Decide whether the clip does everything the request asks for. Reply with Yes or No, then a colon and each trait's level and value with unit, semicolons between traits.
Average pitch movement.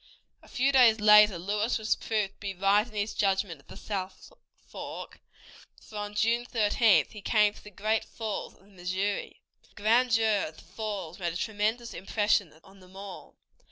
No: narrow, 2.2 semitones